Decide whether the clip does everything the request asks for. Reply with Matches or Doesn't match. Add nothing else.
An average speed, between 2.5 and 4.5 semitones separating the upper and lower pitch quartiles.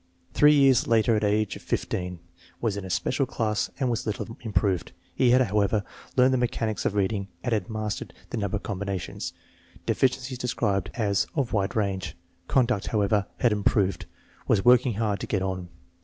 Matches